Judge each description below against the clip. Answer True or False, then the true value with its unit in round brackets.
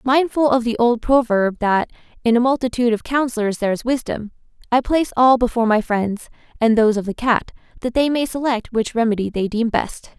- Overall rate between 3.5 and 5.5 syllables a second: False (5.8 syllables/s)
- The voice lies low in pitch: False (235 Hz)